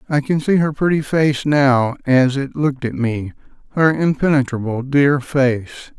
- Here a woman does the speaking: No, male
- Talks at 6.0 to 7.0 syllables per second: No, 4.5 syllables/s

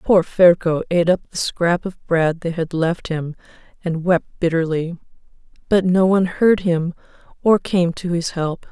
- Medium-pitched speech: Yes, medium, 175 Hz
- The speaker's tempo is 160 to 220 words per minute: Yes, average, 170 wpm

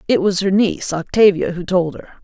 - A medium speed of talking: No, fast, 215 wpm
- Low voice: No, medium, 185 Hz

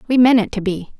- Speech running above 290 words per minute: Yes, fast, 300 wpm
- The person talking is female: Yes, female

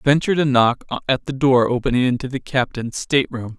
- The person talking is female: No, male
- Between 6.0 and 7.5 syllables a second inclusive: No, 5.8 syllables/s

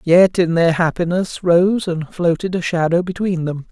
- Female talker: No, male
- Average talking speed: Yes, average, 180 wpm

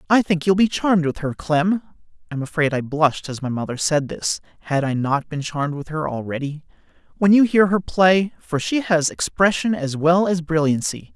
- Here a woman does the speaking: No, male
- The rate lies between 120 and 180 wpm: No, average, 195 wpm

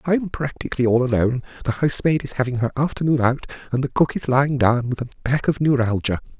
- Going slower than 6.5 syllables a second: No, 6.6 syllables/s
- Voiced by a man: Yes, male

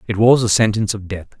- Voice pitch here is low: Yes, low, 105 Hz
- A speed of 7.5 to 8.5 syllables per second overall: No, 7.0 syllables/s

